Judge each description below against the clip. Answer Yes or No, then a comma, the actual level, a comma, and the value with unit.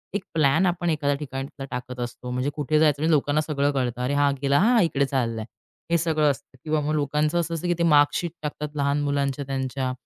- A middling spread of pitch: No, narrow, 2.3 semitones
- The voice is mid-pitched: Yes, medium, 145 Hz